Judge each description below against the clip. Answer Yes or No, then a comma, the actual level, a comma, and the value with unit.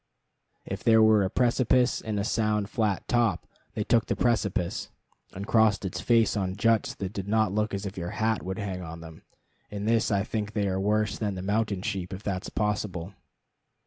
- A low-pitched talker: Yes, low, 105 Hz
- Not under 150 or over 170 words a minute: No, fast, 205 wpm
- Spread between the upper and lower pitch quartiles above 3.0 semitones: No, narrow, 2.4 semitones